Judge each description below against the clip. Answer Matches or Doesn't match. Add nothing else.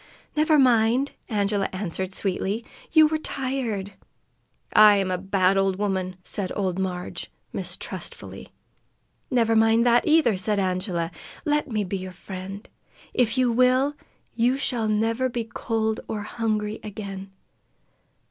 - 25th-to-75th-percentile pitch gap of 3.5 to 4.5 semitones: Matches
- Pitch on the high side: Matches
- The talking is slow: Matches